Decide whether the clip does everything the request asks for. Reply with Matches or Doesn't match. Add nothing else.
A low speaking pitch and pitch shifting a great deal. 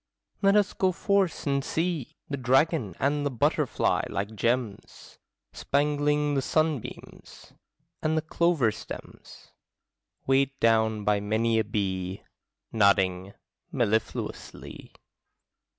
Matches